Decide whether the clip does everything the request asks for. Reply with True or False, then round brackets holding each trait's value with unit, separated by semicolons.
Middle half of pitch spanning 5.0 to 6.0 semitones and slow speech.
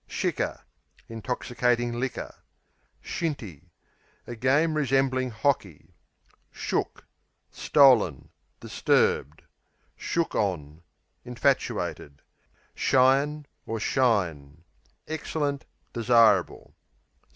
True (5.3 semitones; 65 wpm)